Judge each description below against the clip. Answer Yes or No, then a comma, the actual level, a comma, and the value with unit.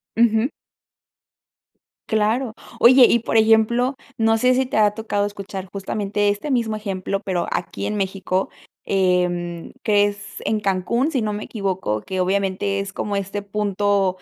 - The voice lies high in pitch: Yes, high, 205 Hz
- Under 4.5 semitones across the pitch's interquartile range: Yes, narrow, 2.4 semitones